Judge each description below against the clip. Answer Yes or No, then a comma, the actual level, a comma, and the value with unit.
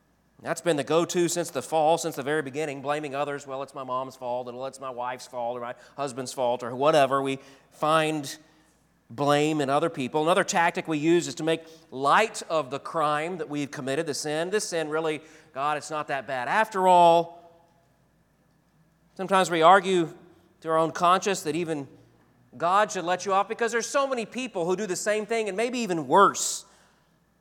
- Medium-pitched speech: Yes, medium, 160 Hz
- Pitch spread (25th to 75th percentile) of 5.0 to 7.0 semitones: No, average, 3.9 semitones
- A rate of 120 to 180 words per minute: No, average, 195 wpm